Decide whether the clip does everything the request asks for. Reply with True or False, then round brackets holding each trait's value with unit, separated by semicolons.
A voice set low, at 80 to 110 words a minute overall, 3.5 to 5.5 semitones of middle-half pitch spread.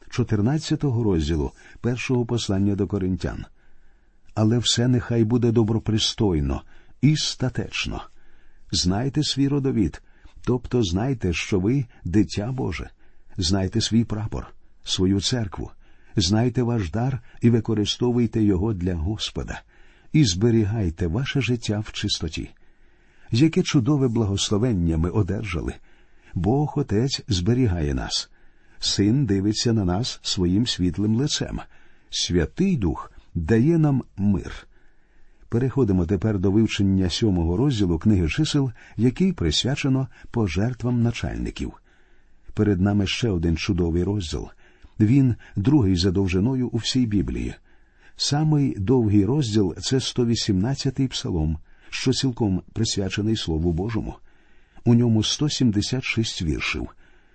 True (110 Hz; 105 wpm; 4.8 semitones)